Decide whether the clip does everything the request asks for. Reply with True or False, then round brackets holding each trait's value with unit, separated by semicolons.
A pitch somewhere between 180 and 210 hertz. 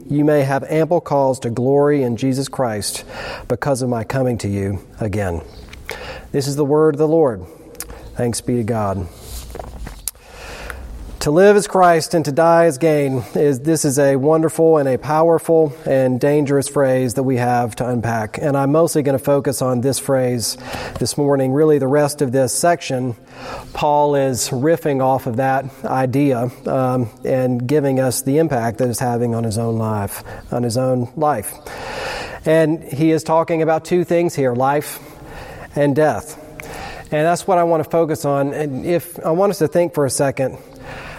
False (140 Hz)